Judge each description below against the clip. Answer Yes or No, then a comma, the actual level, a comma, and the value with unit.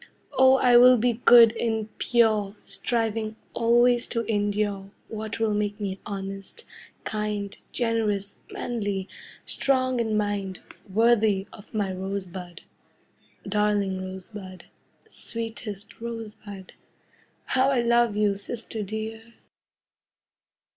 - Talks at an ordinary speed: No, slow, 105 wpm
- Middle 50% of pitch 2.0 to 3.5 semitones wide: Yes, narrow, 2.6 semitones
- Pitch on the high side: Yes, high, 215 Hz